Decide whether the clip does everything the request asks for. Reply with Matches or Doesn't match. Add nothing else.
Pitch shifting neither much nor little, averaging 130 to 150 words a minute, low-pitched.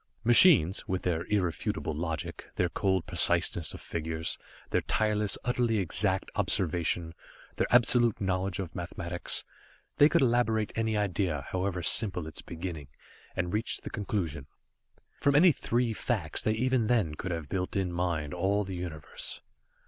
Matches